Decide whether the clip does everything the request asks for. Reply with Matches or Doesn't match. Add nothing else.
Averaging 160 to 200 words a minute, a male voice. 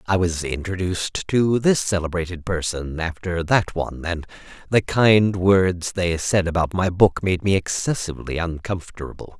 Doesn't match